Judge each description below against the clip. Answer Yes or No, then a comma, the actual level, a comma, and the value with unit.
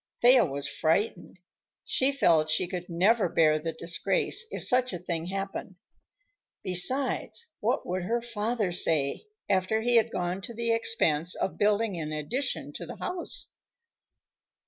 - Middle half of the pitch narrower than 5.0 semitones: No, wide, 5.6 semitones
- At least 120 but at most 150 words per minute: Yes, average, 145 wpm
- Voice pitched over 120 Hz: Yes, high, 190 Hz